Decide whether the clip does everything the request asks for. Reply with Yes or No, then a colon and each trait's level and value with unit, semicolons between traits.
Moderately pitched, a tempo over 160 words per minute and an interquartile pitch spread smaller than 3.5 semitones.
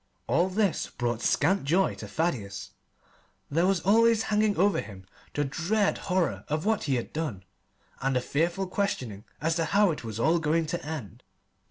No: medium, 165 Hz; average, 175 wpm; wide, 6.6 semitones